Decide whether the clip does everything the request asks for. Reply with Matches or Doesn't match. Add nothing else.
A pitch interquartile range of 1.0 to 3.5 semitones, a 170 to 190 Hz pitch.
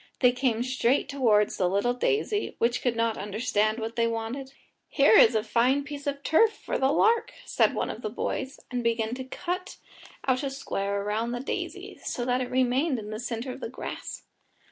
Doesn't match